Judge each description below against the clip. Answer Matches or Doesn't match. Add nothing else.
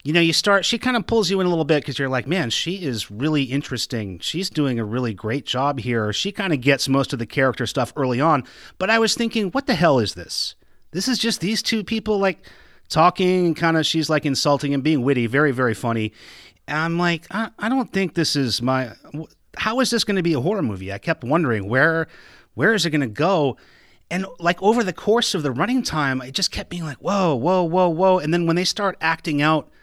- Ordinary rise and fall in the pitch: Doesn't match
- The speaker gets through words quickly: Matches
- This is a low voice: Doesn't match